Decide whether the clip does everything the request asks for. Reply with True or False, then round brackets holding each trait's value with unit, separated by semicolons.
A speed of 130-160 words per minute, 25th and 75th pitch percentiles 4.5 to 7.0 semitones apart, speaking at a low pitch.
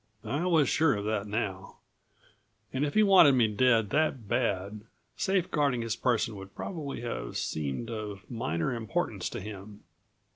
True (155 wpm; 5.6 semitones; 115 Hz)